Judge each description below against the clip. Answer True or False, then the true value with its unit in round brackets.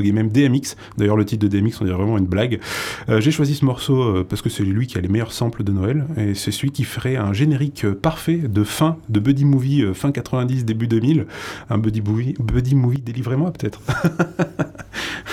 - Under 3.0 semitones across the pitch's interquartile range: False (5.1 semitones)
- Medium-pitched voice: False (120 Hz)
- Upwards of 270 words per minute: False (215 wpm)